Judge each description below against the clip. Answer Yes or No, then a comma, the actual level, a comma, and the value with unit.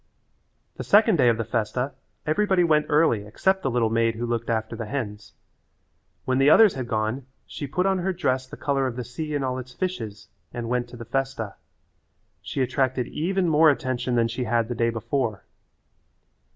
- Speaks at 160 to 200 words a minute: Yes, average, 190 wpm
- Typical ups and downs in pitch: Yes, average, 4.4 semitones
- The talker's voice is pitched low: Yes, low, 125 Hz